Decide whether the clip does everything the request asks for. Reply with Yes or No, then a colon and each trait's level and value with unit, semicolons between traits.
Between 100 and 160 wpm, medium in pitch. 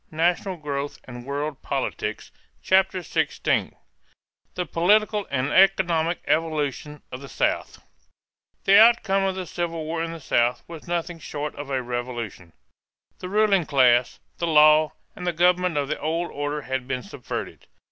Yes: average, 150 wpm; medium, 160 Hz